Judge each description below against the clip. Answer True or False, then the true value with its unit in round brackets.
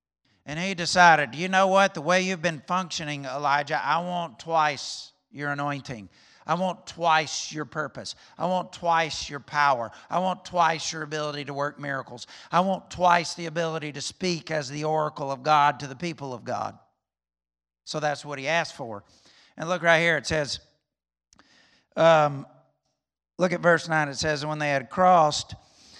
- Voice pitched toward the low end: False (155 Hz)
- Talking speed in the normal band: True (175 wpm)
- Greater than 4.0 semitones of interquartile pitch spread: False (3.2 semitones)